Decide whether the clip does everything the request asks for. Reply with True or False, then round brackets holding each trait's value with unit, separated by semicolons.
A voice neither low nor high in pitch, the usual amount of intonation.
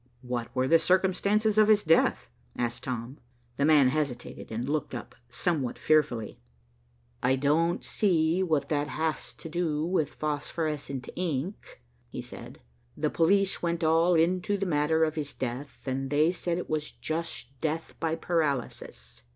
True (155 Hz; 3.8 semitones)